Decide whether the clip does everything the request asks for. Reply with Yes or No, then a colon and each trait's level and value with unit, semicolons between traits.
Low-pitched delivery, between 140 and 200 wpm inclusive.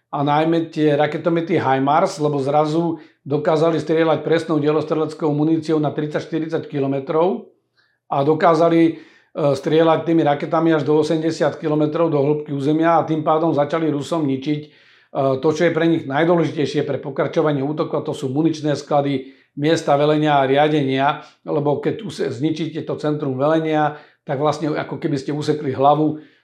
No: medium, 150 Hz; average, 145 wpm